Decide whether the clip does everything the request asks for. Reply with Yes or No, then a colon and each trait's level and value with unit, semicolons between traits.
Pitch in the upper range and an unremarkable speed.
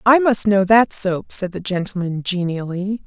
Yes: high, 195 Hz; average, 175 wpm